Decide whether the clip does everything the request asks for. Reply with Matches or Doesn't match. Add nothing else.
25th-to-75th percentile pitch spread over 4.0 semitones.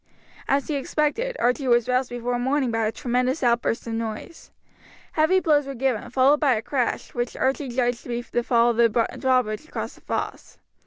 Doesn't match